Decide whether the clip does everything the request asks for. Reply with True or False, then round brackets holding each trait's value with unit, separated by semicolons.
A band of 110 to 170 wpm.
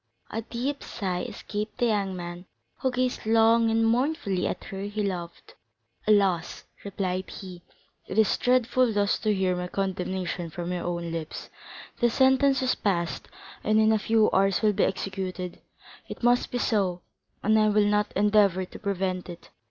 True (165 wpm)